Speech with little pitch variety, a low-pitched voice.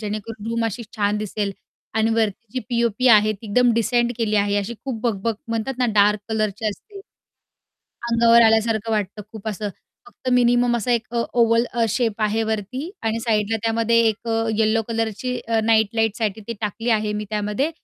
No: narrow, 1.7 semitones; high, 225 Hz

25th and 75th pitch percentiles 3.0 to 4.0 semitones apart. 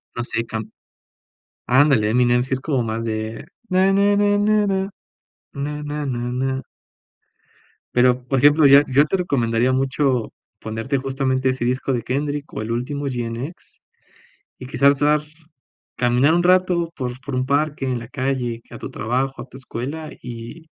Yes: average, 3.4 semitones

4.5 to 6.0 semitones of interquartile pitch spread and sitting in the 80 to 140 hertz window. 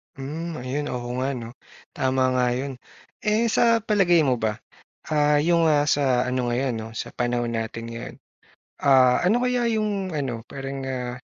Yes: average, 5.2 semitones; low, 135 Hz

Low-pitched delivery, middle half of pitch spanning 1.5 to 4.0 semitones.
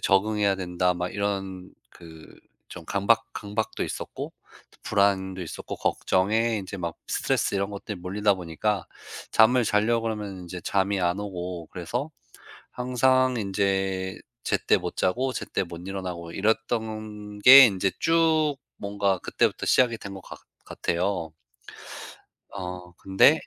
Yes: low, 100 Hz; average, 3.0 semitones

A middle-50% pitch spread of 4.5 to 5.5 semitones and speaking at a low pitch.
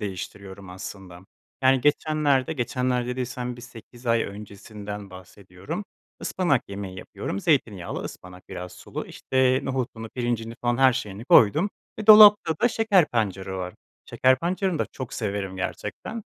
Yes: average, 5.1 semitones; low, 120 Hz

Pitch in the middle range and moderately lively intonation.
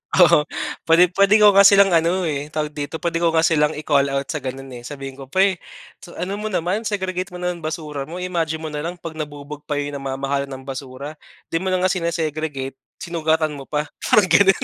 Yes: medium, 160 Hz; average, 3.9 semitones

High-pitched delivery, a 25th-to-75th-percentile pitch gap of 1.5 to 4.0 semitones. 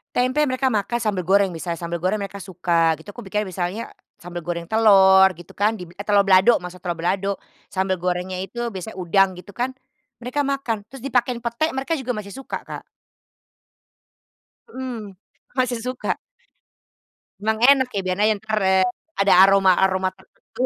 No: high, 200 Hz; average, 4.4 semitones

